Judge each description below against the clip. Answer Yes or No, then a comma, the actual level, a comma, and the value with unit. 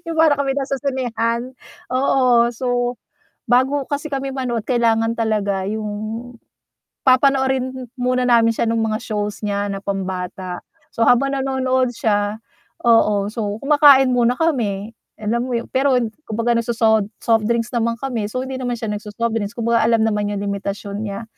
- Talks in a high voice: Yes, high, 235 Hz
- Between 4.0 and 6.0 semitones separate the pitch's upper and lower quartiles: No, average, 3.3 semitones